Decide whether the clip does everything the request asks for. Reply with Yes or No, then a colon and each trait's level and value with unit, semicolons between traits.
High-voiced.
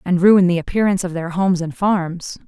No: medium, 180 Hz